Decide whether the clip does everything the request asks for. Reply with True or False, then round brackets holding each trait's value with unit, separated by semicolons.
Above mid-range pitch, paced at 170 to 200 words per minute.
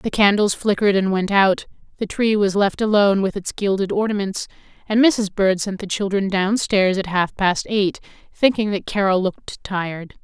True (200 Hz; 190 wpm)